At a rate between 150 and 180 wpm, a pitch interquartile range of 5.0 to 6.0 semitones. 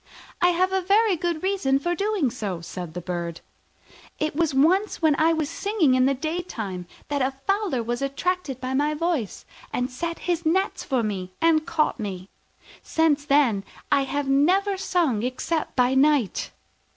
Yes: average, 170 wpm; wide, 5.6 semitones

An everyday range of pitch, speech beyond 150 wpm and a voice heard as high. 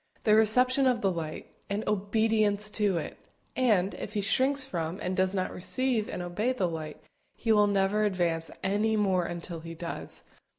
Yes: average, 3.7 semitones; average, 175 wpm; high, 200 Hz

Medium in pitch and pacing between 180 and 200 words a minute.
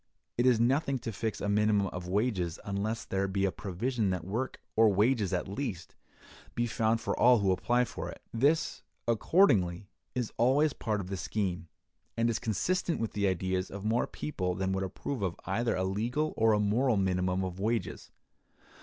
No: low, 105 Hz; average, 185 wpm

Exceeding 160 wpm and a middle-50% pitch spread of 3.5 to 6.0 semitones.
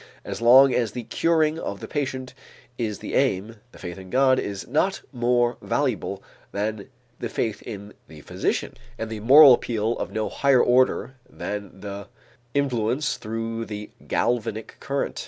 No: average, 155 wpm; average, 3.8 semitones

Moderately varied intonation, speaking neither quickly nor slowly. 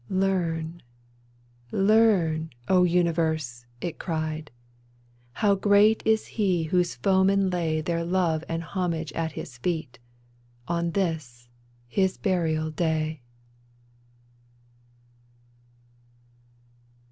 No: average, 3.0 semitones; slow, 100 wpm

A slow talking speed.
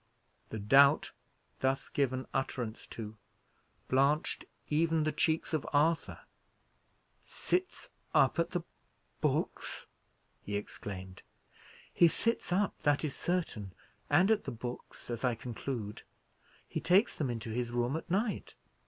Yes: slow, 125 wpm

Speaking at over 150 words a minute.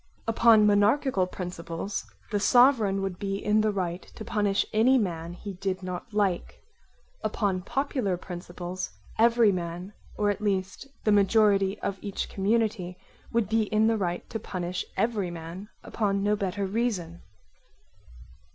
No: average, 140 wpm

